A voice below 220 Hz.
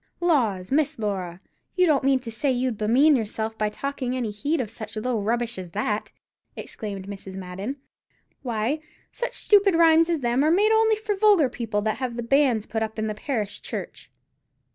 No: high, 240 Hz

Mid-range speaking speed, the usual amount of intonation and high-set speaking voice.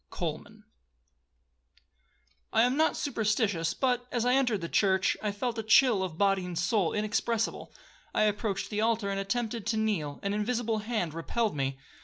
Yes: average, 160 wpm; average, 3.1 semitones; high, 215 Hz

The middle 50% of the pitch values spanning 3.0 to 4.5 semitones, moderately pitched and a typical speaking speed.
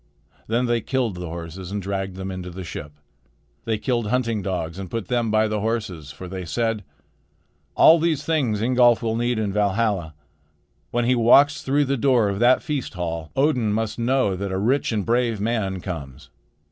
No: average, 4.2 semitones; low, 110 Hz; average, 185 wpm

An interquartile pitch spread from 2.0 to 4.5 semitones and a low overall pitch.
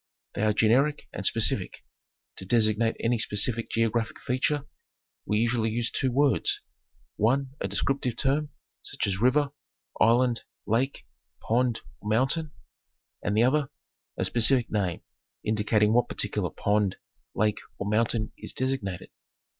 Yes: average, 3.3 semitones; low, 115 Hz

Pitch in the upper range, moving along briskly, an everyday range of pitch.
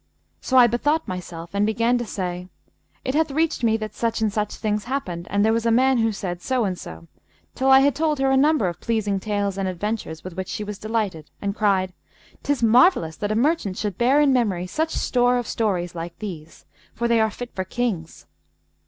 Yes: high, 215 Hz; fast, 215 wpm; average, 4.7 semitones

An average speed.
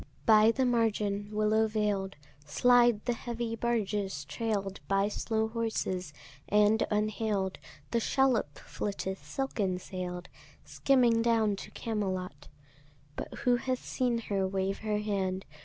No: slow, 125 wpm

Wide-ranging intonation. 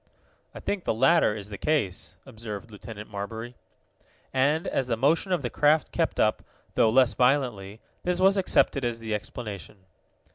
Yes: wide, 5.7 semitones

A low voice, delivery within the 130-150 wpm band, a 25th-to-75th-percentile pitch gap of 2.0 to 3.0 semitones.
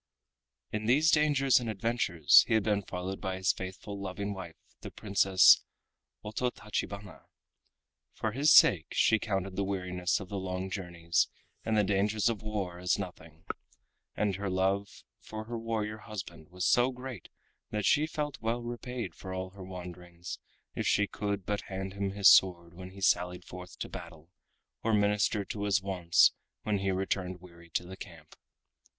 No: very low, 95 Hz; average, 165 wpm; average, 2.7 semitones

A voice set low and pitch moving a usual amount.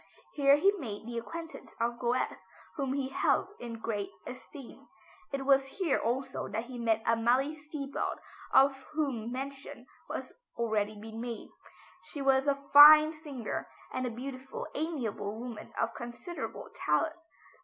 No: very high, 260 Hz; average, 3.5 semitones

